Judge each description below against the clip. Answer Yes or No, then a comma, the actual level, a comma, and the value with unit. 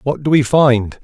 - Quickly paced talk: Yes, fast, 230 wpm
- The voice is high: No, low, 135 Hz